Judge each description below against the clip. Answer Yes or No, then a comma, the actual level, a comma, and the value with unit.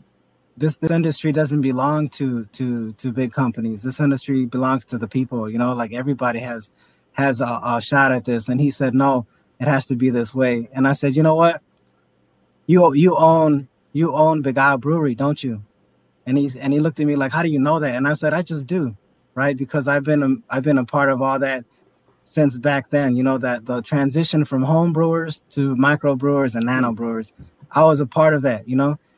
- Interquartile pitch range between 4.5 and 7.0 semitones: No, average, 3.0 semitones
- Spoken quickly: Yes, fast, 220 wpm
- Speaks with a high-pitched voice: No, low, 135 Hz